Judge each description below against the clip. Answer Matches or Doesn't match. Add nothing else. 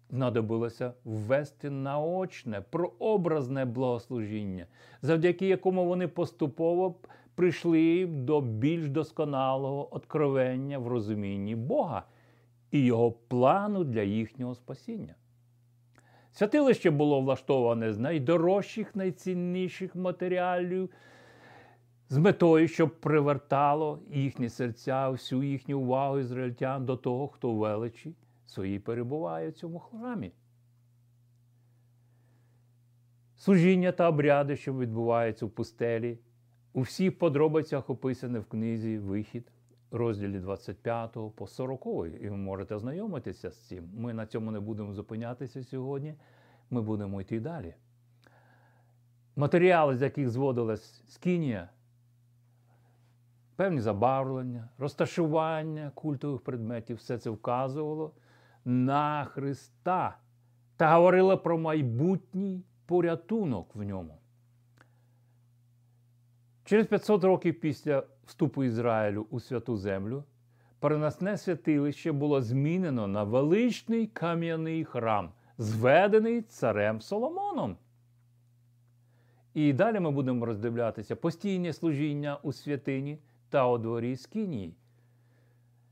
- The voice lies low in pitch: Matches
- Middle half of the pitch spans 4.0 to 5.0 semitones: Matches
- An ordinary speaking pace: Doesn't match